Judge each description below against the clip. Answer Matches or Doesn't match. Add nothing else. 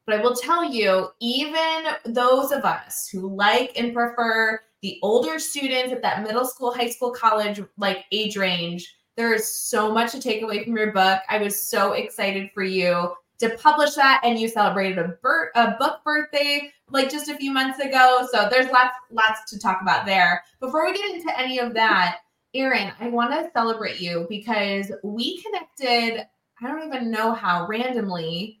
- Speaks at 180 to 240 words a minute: Matches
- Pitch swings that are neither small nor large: Matches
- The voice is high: Matches